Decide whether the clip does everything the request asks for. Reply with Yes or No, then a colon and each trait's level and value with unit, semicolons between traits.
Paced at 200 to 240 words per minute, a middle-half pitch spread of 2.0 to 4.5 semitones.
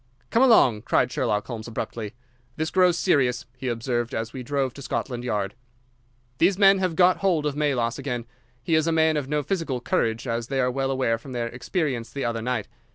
No: fast, 205 wpm; average, 5.1 semitones